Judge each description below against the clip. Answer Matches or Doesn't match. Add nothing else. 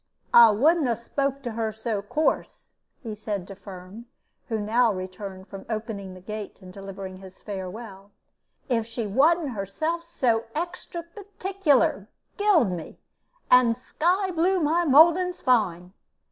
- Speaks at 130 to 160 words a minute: Matches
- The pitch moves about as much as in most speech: Doesn't match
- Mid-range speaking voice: Doesn't match